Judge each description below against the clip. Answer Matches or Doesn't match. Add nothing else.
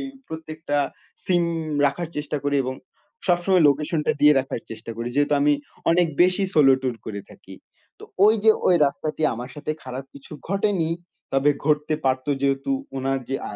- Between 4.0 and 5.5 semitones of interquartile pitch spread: Doesn't match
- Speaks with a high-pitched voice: Doesn't match